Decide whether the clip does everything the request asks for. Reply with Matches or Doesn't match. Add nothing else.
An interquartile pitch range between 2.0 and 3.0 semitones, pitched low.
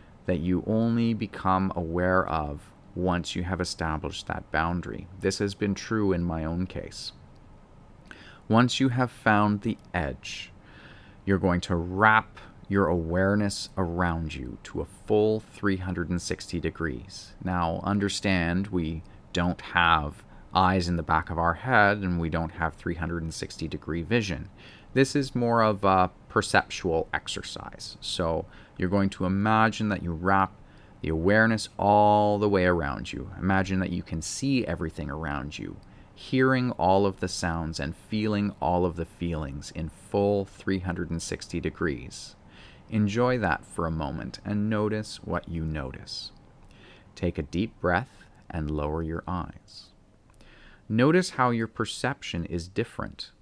Doesn't match